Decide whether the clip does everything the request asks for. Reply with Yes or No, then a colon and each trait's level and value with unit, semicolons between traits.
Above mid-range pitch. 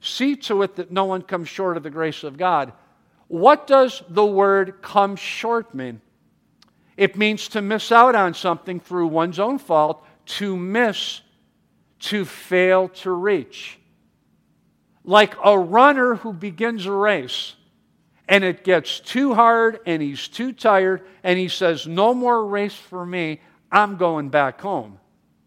Yes: high, 195 Hz